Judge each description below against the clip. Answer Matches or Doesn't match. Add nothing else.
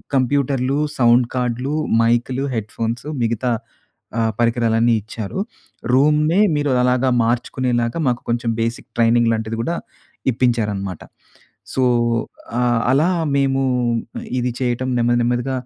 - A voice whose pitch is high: Doesn't match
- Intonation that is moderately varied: Doesn't match